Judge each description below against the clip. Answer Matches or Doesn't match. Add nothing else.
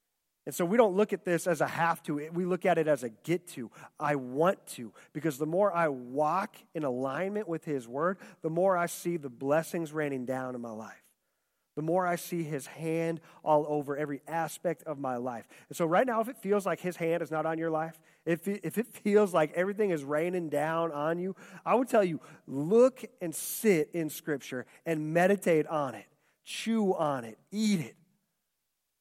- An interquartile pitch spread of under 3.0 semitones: Doesn't match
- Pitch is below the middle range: Doesn't match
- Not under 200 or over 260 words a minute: Matches